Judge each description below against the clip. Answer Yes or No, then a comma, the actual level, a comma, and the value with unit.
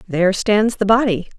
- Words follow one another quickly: No, average, 175 wpm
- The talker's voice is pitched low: No, high, 205 Hz